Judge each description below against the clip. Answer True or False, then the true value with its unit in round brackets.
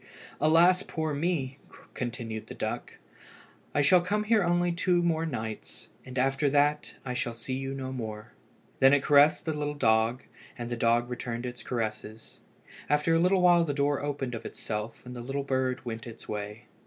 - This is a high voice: False (135 Hz)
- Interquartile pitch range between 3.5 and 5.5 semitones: True (4.7 semitones)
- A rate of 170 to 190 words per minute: True (180 wpm)